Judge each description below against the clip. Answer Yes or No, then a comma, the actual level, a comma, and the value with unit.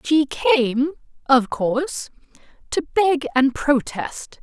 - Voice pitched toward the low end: No, very high, 280 Hz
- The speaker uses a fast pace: No, slow, 110 wpm